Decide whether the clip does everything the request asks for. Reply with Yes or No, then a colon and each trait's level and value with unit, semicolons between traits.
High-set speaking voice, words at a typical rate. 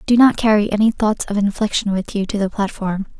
No: high, 205 Hz; fast, 225 wpm